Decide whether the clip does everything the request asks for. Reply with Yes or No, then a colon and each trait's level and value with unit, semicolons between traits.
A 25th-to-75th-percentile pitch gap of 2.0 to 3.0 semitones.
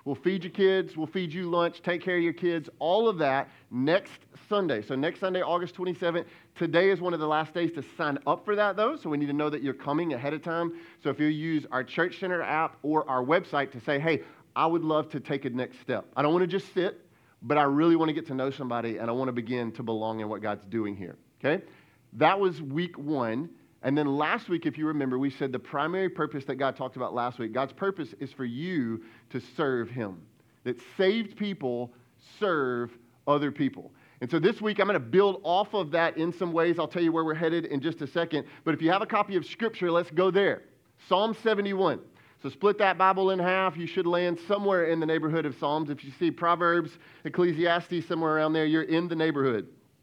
No: average, 4.4 semitones